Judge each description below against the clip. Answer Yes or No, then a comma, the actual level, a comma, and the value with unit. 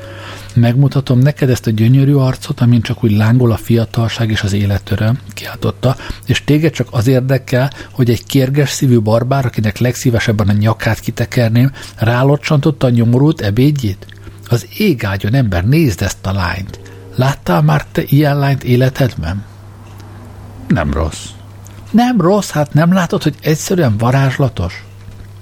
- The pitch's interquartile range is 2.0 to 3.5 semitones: No, average, 4.9 semitones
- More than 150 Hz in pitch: No, low, 120 Hz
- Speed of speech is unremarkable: Yes, average, 135 wpm